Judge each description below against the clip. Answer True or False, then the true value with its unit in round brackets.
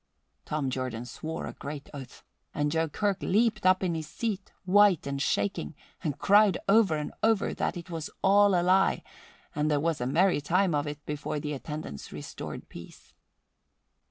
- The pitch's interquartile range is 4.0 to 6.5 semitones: True (4.9 semitones)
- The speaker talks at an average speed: True (175 wpm)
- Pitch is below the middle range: False (160 Hz)